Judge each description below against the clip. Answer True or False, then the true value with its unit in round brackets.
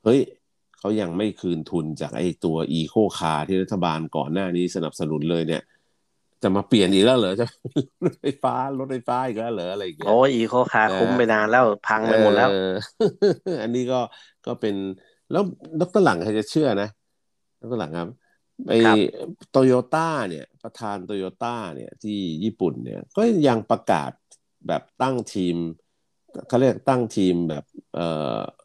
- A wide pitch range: True (6.1 semitones)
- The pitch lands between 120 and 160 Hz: False (105 Hz)